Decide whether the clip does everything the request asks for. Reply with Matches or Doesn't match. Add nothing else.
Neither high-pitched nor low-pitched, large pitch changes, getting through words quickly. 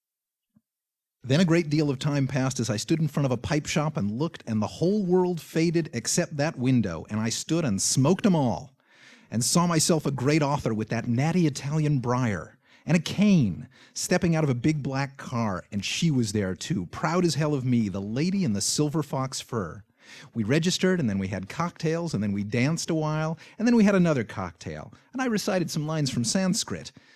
Matches